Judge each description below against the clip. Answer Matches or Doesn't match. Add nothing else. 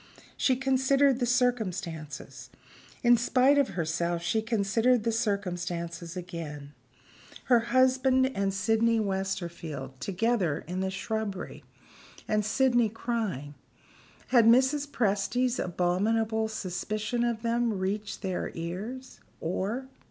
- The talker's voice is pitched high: Matches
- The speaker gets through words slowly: Matches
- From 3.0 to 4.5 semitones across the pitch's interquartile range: Doesn't match